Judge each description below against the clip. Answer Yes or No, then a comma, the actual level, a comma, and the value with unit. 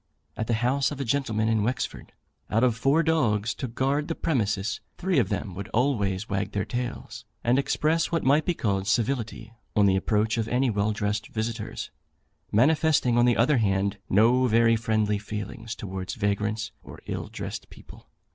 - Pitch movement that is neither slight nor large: Yes, average, 3.7 semitones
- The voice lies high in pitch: No, low, 115 Hz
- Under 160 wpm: No, average, 180 wpm